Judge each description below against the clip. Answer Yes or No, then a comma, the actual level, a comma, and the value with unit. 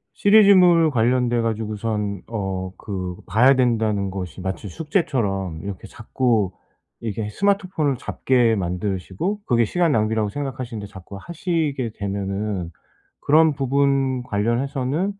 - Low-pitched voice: Yes, low, 115 Hz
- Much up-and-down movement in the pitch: Yes, wide, 5.7 semitones